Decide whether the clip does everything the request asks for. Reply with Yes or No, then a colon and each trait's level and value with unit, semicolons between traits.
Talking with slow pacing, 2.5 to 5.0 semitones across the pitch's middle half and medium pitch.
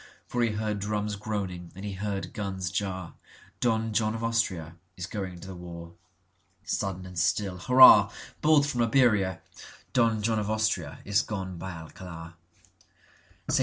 No: slow, 125 wpm; average, 3.4 semitones; low, 100 Hz